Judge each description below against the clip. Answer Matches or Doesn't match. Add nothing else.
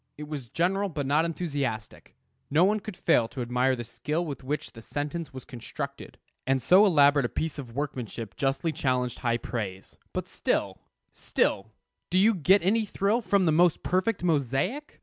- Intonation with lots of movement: Matches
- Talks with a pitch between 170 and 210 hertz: Doesn't match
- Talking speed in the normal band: Matches